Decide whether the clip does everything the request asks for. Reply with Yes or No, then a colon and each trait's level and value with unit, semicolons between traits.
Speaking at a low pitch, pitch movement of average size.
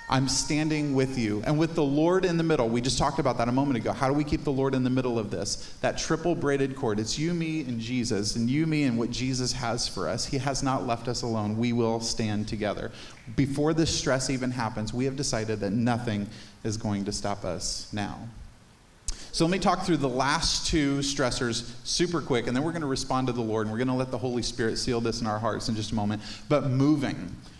Yes: low, 125 Hz; average, 3.9 semitones